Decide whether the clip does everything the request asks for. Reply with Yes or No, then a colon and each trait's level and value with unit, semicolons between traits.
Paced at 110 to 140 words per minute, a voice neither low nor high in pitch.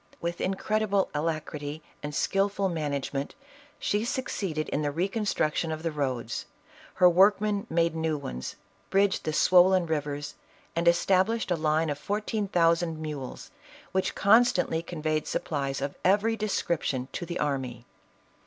Yes: slow, 135 wpm; medium, 165 Hz